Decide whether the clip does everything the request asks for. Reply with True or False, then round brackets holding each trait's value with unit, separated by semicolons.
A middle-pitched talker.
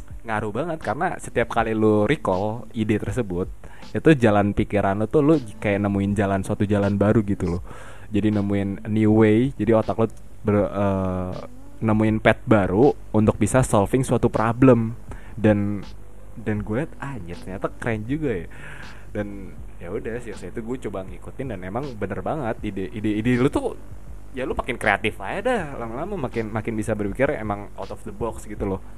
False (110 Hz)